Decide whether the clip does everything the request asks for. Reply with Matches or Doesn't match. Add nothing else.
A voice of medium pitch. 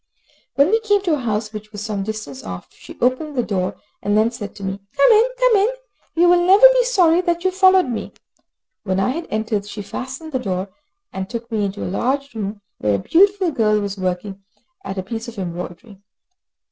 Doesn't match